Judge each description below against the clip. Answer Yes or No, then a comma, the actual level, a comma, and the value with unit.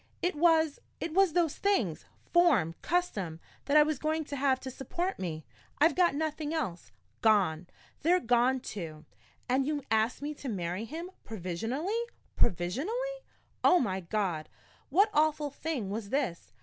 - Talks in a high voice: Yes, very high, 275 Hz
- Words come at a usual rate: Yes, average, 150 wpm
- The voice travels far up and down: Yes, wide, 8.3 semitones